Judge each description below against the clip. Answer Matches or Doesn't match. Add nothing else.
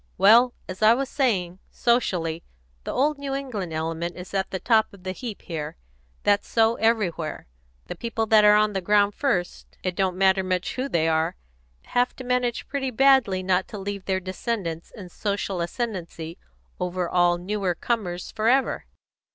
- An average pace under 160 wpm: Doesn't match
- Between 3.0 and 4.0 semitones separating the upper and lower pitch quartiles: Doesn't match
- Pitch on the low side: Doesn't match